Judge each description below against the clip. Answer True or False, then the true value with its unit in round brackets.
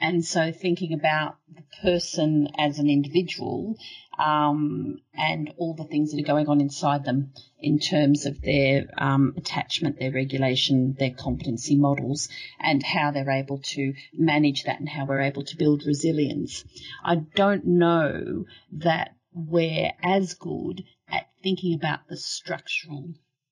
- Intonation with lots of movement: False (3.1 semitones)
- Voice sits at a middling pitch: True (150 Hz)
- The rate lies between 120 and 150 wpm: True (145 wpm)